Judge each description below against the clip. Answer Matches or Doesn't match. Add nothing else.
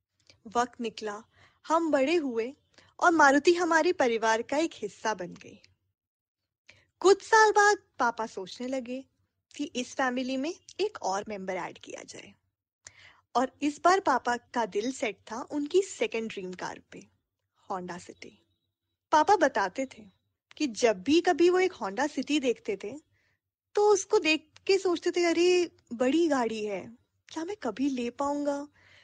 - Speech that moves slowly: Doesn't match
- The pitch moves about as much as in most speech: Doesn't match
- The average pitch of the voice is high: Matches